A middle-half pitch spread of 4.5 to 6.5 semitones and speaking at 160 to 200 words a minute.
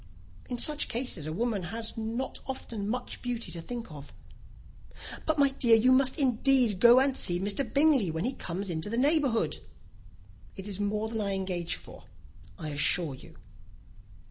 Yes: wide, 5.6 semitones; average, 170 wpm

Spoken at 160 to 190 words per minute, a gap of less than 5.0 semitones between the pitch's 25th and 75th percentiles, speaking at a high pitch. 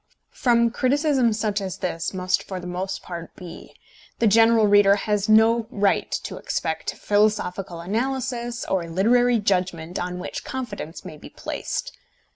No: average, 145 wpm; average, 4.3 semitones; high, 205 Hz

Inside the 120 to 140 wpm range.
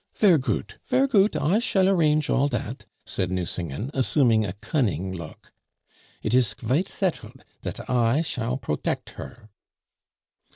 Yes: slow, 135 wpm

